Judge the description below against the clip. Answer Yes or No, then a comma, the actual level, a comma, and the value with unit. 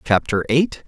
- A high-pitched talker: No, low, 120 Hz